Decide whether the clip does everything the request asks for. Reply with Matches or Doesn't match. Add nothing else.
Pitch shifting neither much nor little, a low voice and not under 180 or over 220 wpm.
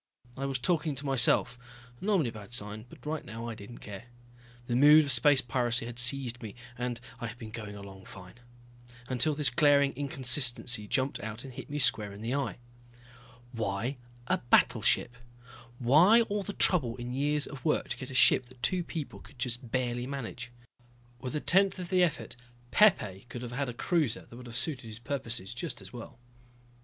Matches